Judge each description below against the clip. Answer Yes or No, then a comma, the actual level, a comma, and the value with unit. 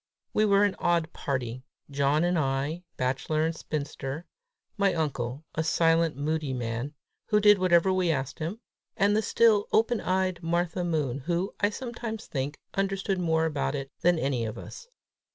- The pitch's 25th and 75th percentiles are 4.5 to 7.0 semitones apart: Yes, average, 5.2 semitones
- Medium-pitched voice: Yes, medium, 165 Hz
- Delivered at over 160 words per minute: Yes, average, 170 wpm